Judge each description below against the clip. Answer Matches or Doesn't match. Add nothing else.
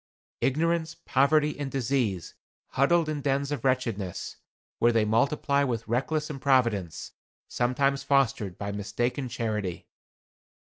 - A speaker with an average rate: Doesn't match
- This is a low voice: Matches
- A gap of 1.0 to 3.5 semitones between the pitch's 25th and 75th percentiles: Doesn't match